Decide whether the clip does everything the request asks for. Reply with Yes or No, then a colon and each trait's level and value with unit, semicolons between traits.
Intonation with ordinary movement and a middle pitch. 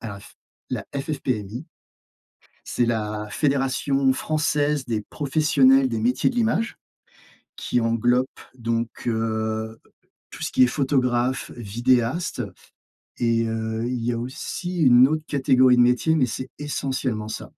No: average, 3.2 semitones; low, 125 Hz